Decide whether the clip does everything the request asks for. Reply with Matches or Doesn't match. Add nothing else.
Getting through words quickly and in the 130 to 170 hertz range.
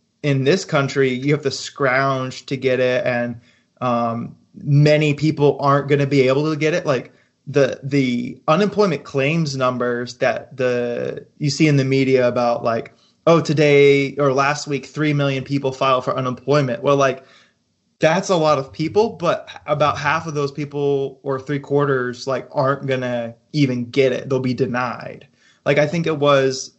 Doesn't match